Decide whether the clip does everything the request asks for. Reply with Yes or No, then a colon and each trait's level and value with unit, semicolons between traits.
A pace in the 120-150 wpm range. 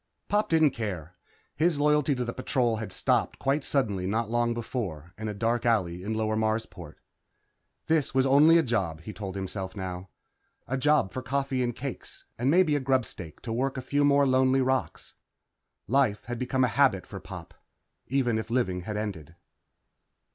No: average, 175 wpm